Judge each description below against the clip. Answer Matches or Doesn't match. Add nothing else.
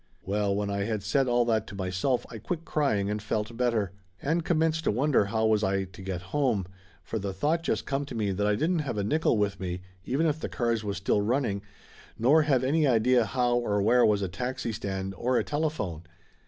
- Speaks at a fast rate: Matches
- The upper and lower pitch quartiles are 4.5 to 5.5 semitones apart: Matches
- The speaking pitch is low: Matches